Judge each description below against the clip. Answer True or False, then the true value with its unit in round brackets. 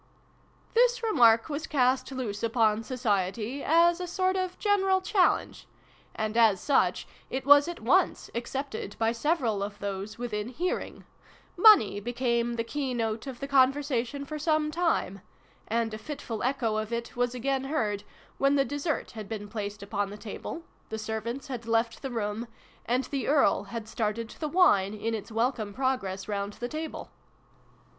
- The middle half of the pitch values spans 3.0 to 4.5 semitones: False (4.9 semitones)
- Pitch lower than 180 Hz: False (240 Hz)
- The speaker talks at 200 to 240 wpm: False (165 wpm)